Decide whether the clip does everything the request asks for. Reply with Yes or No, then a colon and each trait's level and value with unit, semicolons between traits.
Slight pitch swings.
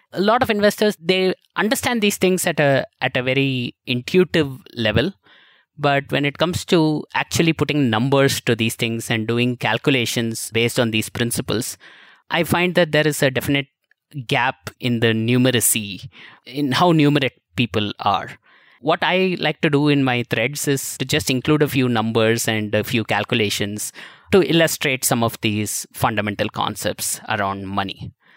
No: average, 5.0 semitones